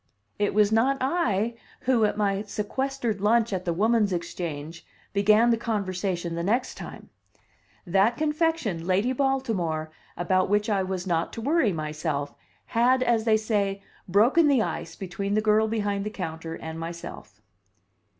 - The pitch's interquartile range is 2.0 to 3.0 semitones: No, average, 4.6 semitones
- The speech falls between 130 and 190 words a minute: Yes, average, 150 wpm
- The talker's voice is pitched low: No, high, 205 Hz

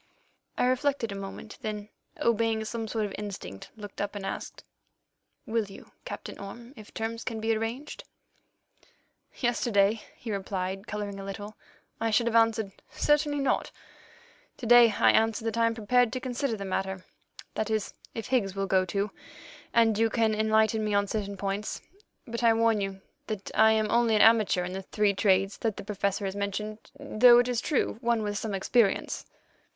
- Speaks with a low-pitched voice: No, high, 220 Hz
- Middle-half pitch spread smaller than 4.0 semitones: Yes, narrow, 2.4 semitones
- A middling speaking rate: Yes, average, 175 wpm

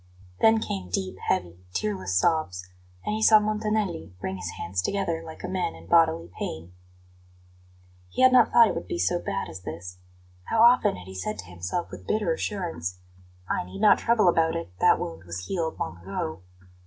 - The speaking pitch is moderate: Yes, medium, 155 Hz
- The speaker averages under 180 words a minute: No, average, 190 wpm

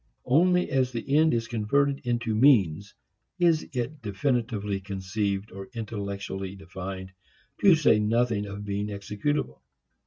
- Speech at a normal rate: No, slow, 125 wpm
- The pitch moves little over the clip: No, average, 4.8 semitones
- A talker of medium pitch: No, low, 110 Hz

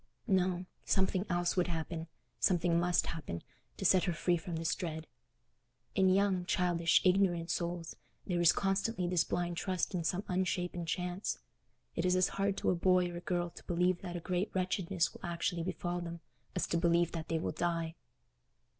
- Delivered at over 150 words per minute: Yes, average, 170 wpm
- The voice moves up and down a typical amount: No, narrow, 1.4 semitones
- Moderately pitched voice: Yes, medium, 175 Hz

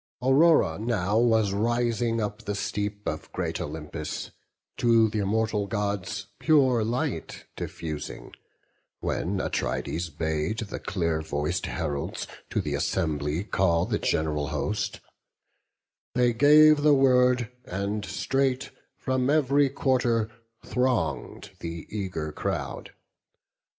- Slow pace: Yes, slow, 110 wpm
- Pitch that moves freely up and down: Yes, wide, 7.0 semitones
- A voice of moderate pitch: No, low, 110 Hz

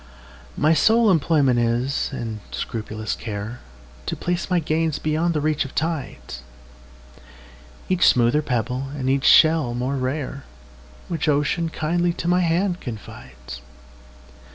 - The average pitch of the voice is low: Yes, low, 130 Hz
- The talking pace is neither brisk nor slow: No, slow, 115 wpm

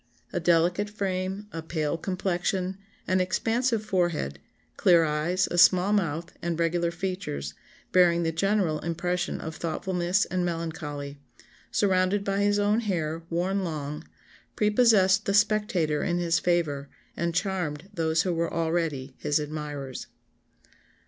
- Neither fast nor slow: No, slow, 130 wpm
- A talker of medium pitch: Yes, medium, 175 Hz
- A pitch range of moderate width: Yes, average, 3.1 semitones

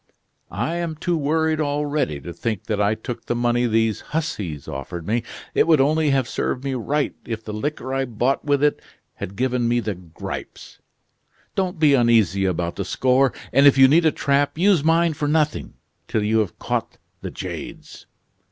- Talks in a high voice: No, low, 130 Hz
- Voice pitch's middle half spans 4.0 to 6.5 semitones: Yes, wide, 5.5 semitones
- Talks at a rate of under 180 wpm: No, average, 185 wpm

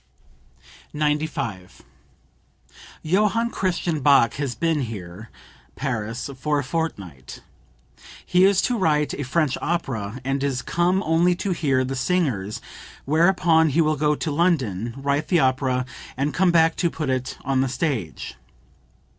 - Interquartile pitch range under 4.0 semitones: No, average, 4.6 semitones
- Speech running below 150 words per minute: Yes, average, 140 wpm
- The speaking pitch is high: No, medium, 145 Hz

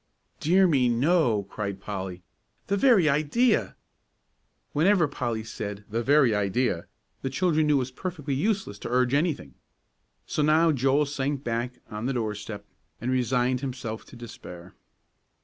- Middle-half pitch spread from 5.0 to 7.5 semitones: Yes, wide, 5.4 semitones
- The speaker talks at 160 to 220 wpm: No, average, 145 wpm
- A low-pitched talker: Yes, low, 130 Hz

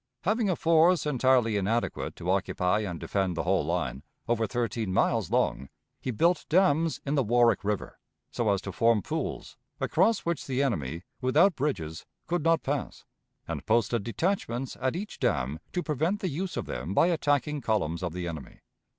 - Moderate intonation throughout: No, wide, 8.6 semitones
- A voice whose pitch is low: Yes, low, 120 Hz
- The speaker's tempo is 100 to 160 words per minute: No, average, 175 wpm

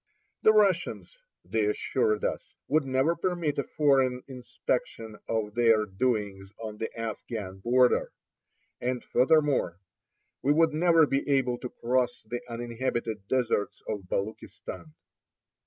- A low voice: Yes, low, 125 Hz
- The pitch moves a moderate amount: Yes, average, 4.8 semitones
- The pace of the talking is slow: Yes, slow, 125 wpm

